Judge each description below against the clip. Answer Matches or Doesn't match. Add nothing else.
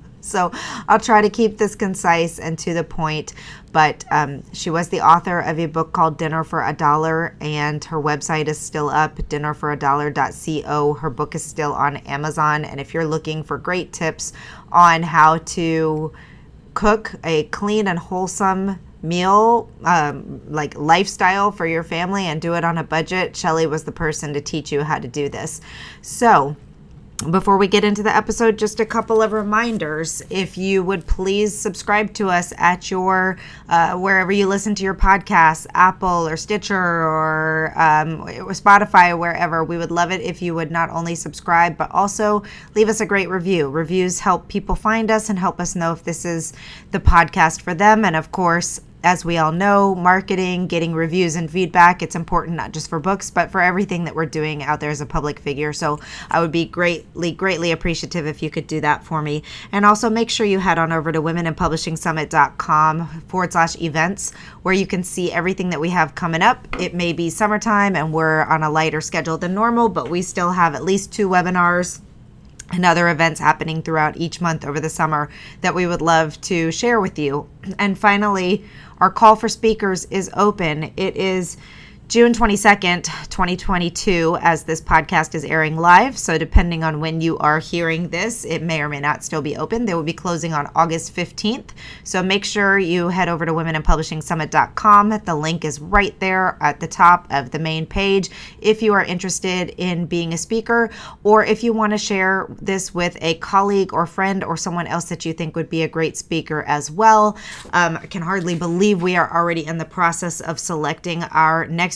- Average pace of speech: Matches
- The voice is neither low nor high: Matches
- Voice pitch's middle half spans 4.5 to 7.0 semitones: Doesn't match